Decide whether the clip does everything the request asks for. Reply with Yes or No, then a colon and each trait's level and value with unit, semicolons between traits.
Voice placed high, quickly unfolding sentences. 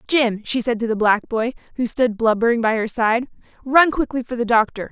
Yes: high, 235 Hz; fast, 220 wpm